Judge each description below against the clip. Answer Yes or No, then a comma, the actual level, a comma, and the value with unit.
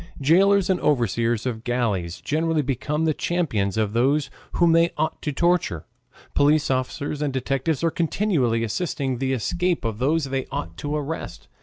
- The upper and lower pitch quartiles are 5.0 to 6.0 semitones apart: Yes, average, 5.3 semitones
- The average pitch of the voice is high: No, medium, 140 Hz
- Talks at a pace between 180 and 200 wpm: No, average, 160 wpm